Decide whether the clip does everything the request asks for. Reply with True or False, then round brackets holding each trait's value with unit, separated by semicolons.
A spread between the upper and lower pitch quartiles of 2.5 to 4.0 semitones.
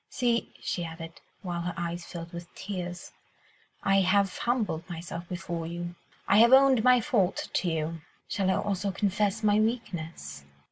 True (3.6 semitones)